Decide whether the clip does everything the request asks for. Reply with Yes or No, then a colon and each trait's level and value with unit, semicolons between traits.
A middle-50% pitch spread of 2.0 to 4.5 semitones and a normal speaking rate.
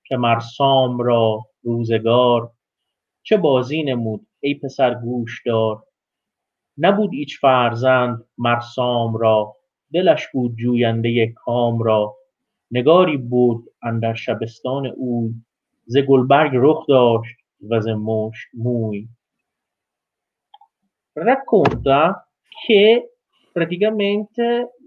No: average, 4.2 semitones; slow, 85 wpm